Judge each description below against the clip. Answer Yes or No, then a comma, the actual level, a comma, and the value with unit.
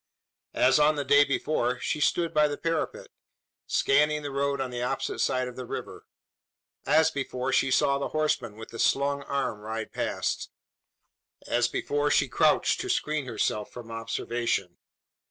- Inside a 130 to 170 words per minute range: Yes, average, 160 wpm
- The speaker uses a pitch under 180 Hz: Yes, low, 135 Hz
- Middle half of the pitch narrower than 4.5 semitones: Yes, average, 3.4 semitones